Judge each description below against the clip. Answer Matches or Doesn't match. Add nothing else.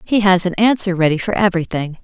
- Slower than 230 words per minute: Matches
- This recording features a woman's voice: Matches